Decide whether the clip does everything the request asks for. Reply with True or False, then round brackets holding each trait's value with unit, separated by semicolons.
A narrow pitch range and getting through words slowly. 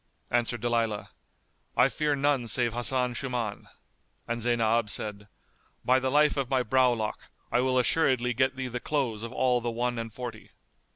False (2.0 semitones; 165 wpm)